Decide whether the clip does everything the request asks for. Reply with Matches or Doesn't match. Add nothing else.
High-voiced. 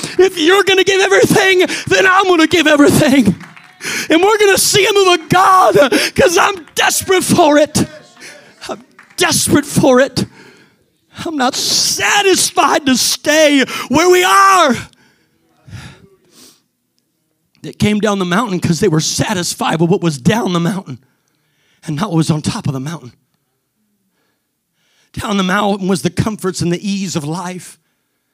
Matches